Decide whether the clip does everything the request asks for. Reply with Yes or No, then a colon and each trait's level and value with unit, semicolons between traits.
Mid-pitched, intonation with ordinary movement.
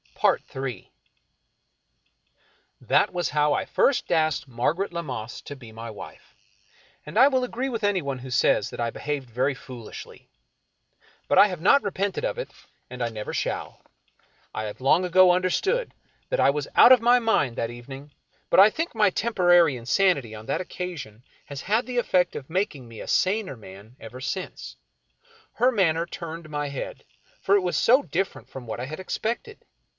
No: medium, 165 Hz; wide, 7.8 semitones